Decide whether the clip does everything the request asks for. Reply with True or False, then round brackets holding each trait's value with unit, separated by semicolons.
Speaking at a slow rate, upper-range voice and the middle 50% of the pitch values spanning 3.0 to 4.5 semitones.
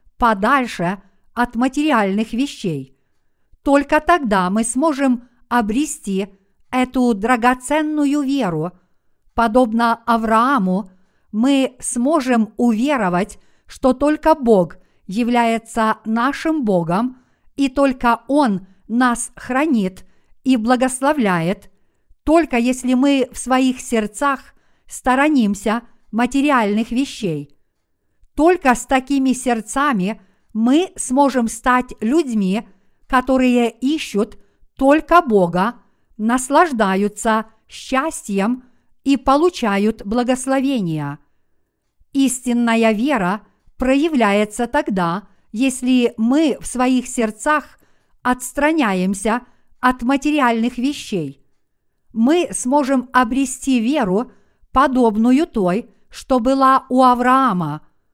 True (80 wpm; 245 Hz; 4.2 semitones)